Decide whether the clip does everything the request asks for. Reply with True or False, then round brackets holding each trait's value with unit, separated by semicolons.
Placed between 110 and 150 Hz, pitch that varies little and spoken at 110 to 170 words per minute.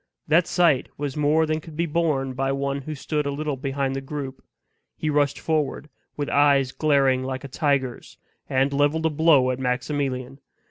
False (140 Hz; 2.2 semitones; 180 wpm)